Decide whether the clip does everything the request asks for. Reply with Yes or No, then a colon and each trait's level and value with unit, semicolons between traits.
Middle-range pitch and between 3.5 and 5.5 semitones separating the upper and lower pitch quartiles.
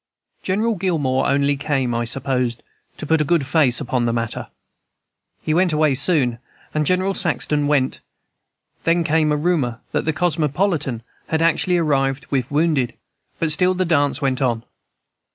Yes: medium, 150 Hz; average, 4.1 semitones